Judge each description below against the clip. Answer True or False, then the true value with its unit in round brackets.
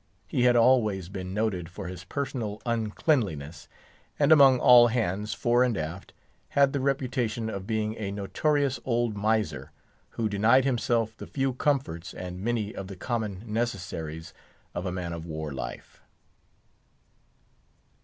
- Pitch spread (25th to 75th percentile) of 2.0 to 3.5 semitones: False (5.0 semitones)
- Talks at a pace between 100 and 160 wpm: True (145 wpm)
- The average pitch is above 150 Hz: False (110 Hz)